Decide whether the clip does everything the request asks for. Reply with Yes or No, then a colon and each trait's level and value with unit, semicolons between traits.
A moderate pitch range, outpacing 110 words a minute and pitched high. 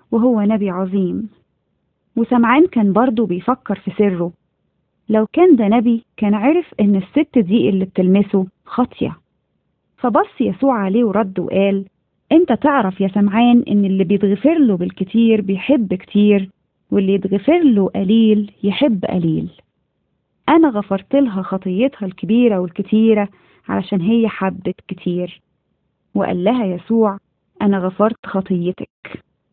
Yes: average, 3.3 semitones; average, 120 wpm; high, 205 Hz